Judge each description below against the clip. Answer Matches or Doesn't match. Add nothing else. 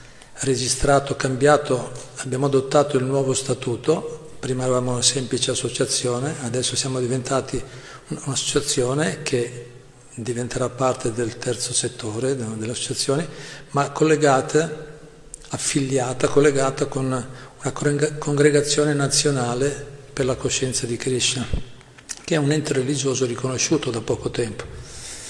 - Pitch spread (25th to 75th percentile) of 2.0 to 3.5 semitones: Matches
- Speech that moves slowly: Matches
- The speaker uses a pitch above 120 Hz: Matches